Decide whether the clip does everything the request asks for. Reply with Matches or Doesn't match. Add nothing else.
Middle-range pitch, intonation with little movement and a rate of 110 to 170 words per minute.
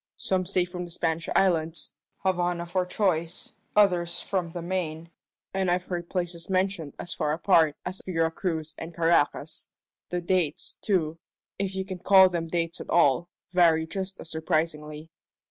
Matches